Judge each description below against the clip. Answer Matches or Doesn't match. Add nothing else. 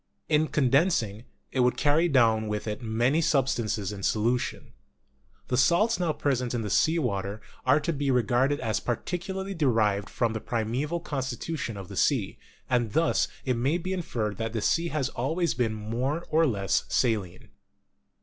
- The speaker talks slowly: Doesn't match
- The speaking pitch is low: Matches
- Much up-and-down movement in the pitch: Matches